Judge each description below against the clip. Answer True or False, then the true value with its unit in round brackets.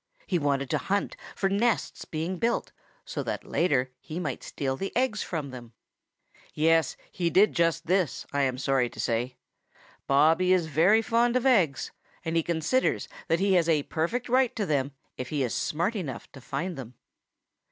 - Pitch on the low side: False (165 Hz)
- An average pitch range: False (5.8 semitones)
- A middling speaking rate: True (180 wpm)